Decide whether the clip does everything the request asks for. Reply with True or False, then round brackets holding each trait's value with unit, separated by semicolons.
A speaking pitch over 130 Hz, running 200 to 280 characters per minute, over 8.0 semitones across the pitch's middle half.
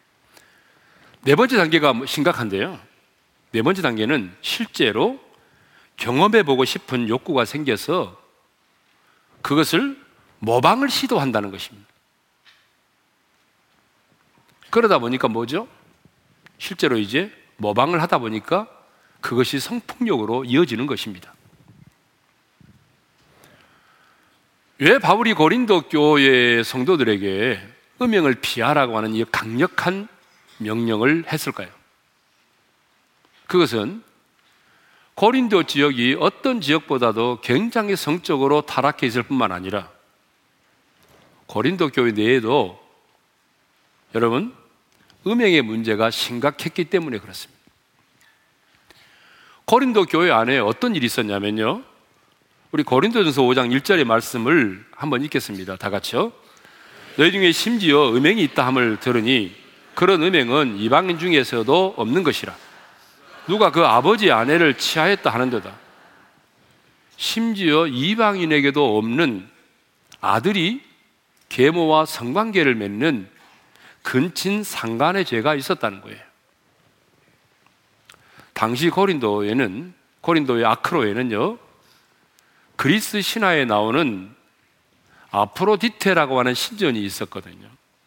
True (140 Hz; 240 characters per minute; 8.4 semitones)